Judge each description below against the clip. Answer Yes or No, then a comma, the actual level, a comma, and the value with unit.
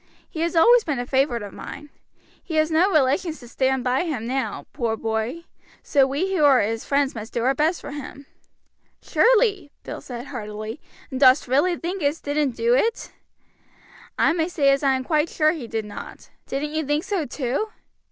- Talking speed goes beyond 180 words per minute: Yes, average, 200 wpm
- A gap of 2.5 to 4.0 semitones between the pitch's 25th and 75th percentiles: No, average, 4.4 semitones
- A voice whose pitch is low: No, very high, 280 Hz